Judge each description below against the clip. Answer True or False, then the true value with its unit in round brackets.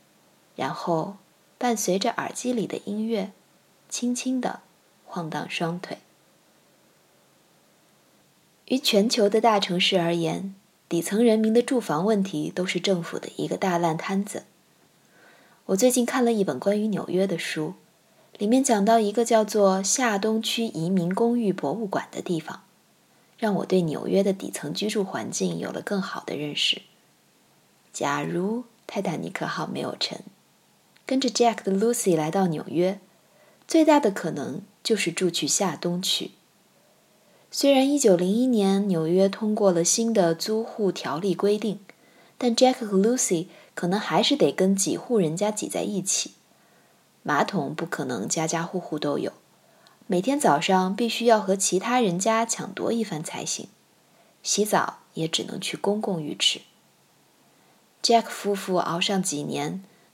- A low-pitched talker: False (200 Hz)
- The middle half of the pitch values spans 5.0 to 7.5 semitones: False (4.1 semitones)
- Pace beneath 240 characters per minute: True (225 characters per minute)